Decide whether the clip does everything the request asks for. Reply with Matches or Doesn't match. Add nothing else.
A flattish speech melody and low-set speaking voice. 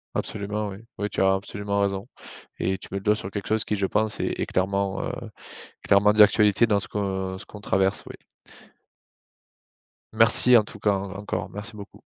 Matches